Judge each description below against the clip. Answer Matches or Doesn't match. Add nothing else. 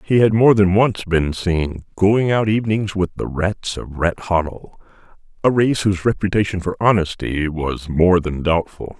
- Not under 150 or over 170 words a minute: Matches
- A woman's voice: Doesn't match